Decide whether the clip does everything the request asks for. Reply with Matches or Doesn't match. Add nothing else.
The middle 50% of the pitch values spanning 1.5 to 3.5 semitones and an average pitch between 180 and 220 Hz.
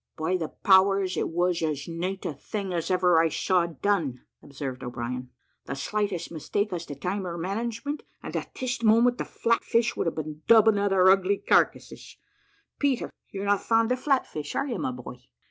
Doesn't match